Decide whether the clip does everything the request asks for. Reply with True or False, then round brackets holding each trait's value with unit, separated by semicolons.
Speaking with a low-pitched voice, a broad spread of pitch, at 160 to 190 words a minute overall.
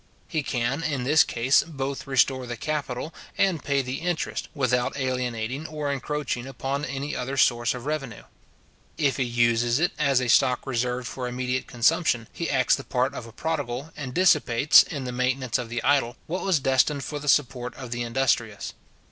False (130 Hz; 2.9 semitones; 180 wpm)